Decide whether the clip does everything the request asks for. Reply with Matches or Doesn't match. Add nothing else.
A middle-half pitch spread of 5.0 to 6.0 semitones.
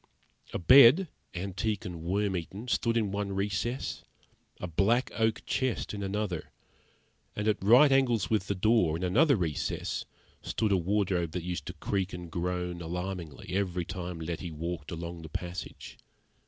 Doesn't match